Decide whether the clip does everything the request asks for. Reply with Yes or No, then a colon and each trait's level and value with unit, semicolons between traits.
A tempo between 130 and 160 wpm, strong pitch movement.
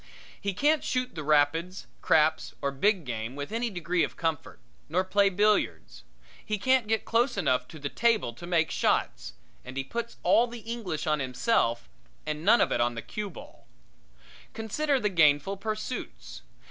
No: average, 170 wpm; wide, 7.3 semitones